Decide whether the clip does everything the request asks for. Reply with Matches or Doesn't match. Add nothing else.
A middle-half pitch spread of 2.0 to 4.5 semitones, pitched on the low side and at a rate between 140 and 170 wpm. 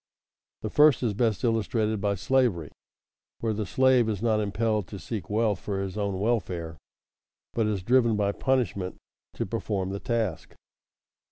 Matches